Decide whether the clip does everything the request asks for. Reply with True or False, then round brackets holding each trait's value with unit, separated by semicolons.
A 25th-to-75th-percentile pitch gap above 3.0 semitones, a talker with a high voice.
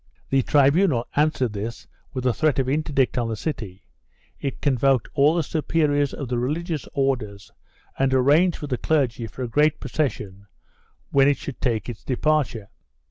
False (3.8 semitones; 135 Hz)